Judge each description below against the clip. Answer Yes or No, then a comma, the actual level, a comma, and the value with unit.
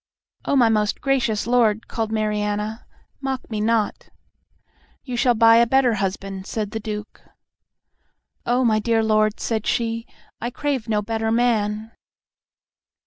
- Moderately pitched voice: No, high, 225 Hz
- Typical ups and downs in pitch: No, narrow, 2.1 semitones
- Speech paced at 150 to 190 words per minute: No, average, 140 wpm